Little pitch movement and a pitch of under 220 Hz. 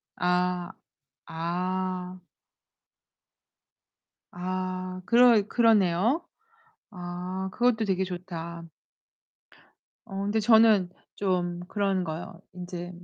Yes: narrow, 2.3 semitones; medium, 185 Hz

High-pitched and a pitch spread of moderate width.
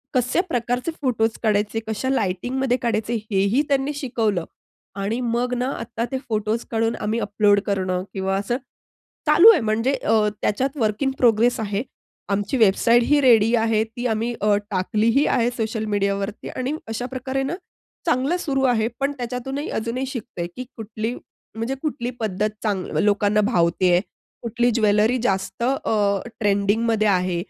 Yes: high, 225 Hz; average, 3.3 semitones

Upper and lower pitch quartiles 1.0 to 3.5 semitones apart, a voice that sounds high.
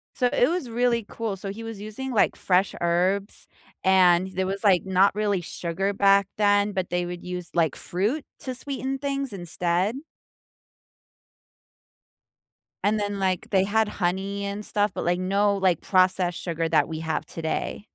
Yes: average, 2.9 semitones; high, 195 Hz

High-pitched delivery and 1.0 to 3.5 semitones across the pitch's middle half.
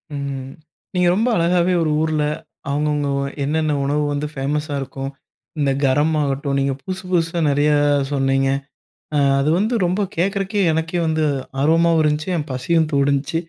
No: medium, 150 Hz; average, 3.1 semitones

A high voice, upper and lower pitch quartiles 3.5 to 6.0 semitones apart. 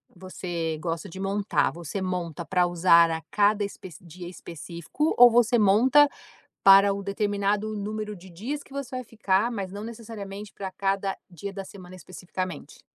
No: high, 195 Hz; average, 3.0 semitones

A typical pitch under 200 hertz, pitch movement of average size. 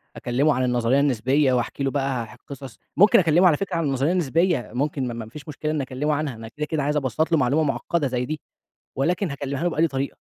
Yes: medium, 140 Hz; average, 3.3 semitones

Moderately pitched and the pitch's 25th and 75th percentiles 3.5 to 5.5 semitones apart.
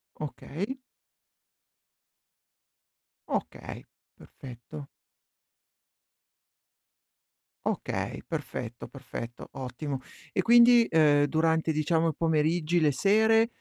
Yes: medium, 160 Hz; average, 5.2 semitones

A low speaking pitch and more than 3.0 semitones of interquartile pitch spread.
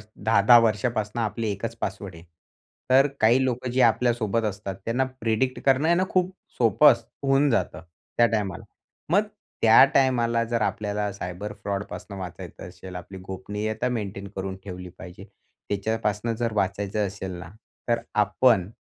Yes: low, 110 Hz; average, 3.4 semitones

